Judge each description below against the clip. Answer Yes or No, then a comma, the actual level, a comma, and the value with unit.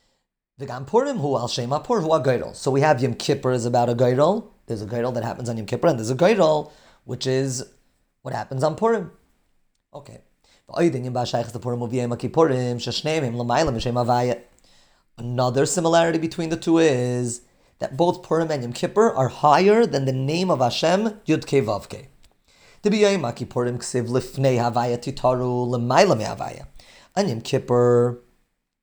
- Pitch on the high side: No, low, 130 Hz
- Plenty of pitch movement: No, average, 4.6 semitones